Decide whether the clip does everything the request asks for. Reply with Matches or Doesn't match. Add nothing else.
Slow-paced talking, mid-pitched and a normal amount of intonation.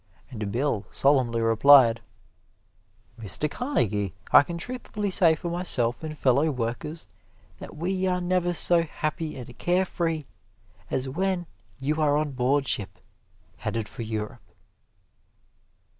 Doesn't match